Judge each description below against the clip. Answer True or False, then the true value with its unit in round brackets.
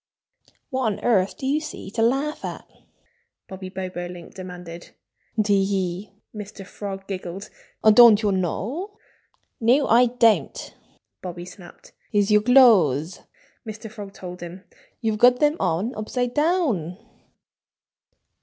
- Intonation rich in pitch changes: False (4.8 semitones)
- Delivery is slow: True (125 wpm)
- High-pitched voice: True (205 Hz)